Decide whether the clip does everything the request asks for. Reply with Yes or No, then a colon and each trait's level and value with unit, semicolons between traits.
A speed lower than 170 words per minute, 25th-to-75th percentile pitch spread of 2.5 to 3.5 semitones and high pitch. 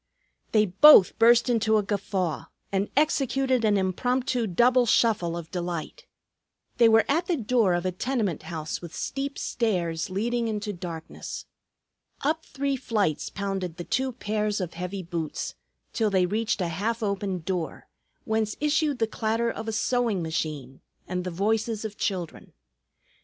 No: average, 150 wpm; average, 4.8 semitones; high, 210 Hz